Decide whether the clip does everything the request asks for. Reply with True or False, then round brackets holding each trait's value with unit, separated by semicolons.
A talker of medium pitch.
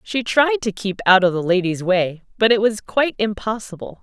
False (205 Hz)